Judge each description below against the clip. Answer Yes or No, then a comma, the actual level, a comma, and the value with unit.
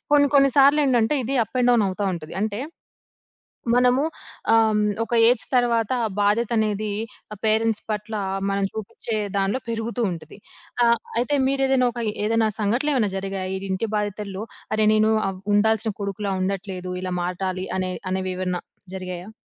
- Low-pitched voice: No, high, 215 Hz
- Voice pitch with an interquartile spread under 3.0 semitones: No, average, 3.5 semitones